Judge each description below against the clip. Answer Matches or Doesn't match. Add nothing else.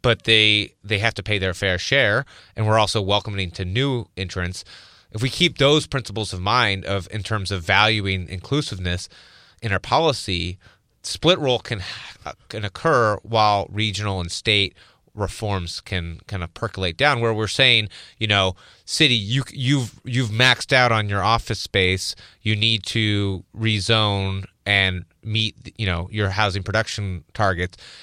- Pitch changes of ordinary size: Matches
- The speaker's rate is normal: Matches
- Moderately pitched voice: Doesn't match